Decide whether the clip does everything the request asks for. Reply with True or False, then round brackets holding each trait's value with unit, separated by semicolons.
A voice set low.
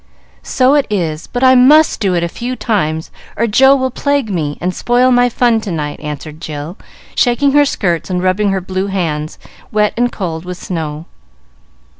False (195 Hz)